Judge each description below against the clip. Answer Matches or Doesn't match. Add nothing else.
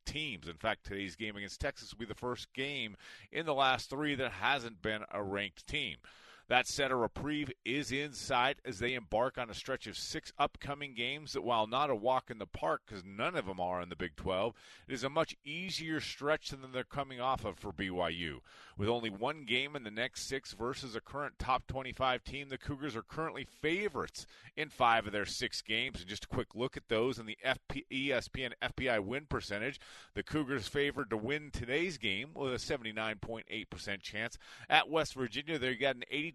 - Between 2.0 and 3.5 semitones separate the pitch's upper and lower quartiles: Doesn't match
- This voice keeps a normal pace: Doesn't match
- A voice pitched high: Doesn't match